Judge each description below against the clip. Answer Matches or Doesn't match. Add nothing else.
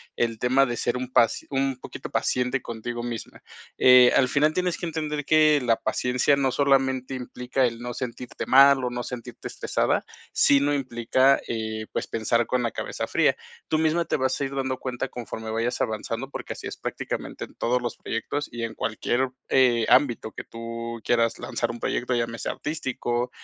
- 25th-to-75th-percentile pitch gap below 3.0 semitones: Matches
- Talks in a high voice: Doesn't match